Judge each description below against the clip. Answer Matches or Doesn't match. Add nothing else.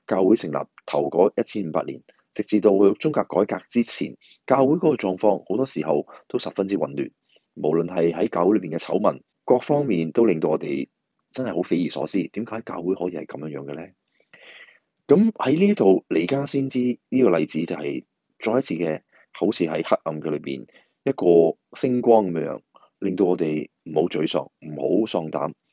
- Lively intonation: Matches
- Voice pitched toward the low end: Matches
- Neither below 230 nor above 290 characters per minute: Matches